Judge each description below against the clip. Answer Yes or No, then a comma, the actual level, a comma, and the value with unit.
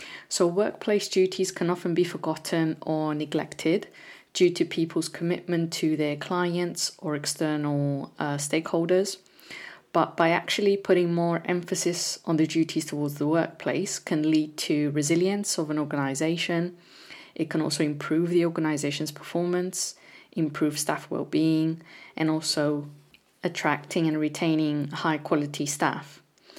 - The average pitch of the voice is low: No, medium, 165 Hz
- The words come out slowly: Yes, slow, 125 wpm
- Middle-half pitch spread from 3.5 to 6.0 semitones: No, narrow, 2.4 semitones